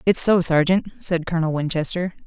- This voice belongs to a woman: Yes, female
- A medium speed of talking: Yes, average, 160 wpm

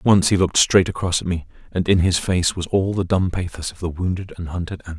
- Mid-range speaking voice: No, very low, 90 Hz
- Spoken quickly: Yes, fast, 265 wpm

